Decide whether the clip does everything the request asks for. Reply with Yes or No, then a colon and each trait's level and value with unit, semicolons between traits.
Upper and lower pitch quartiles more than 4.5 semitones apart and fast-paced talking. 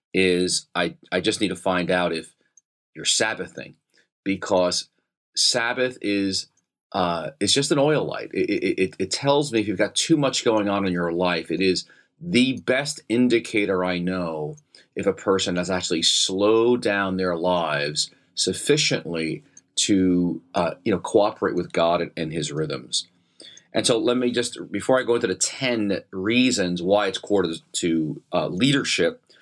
No: average, 5.0 semitones; average, 165 wpm